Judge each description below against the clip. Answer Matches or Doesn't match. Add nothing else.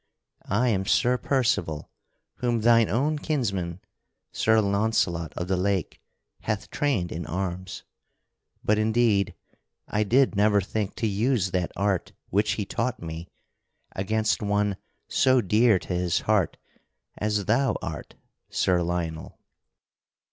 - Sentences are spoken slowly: Matches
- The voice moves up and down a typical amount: Matches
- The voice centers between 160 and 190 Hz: Doesn't match